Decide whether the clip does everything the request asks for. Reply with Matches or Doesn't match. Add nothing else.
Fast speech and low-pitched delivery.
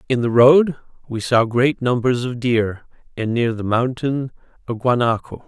Doesn't match